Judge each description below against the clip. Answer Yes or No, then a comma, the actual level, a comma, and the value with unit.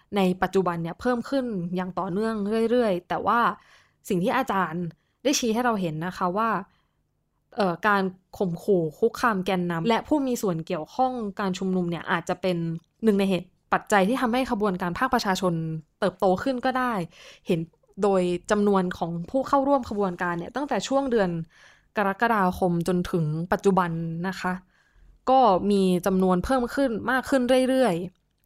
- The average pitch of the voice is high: Yes, high, 195 Hz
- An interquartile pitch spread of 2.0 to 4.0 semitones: No, average, 4.6 semitones